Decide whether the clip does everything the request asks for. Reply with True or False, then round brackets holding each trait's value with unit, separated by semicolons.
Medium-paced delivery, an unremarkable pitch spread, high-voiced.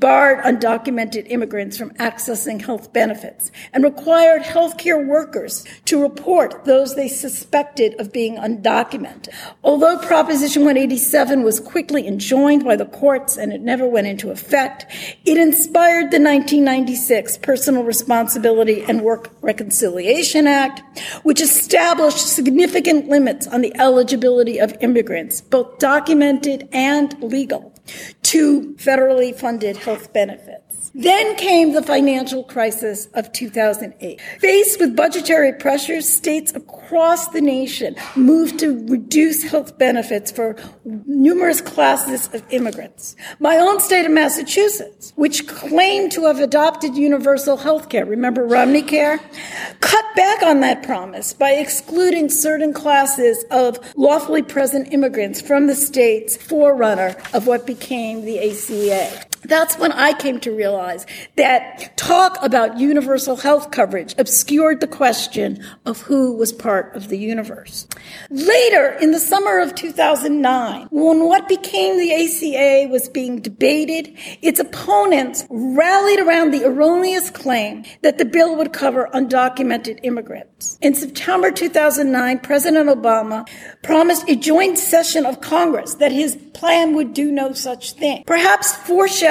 False (130 wpm; 4.3 semitones; 280 Hz)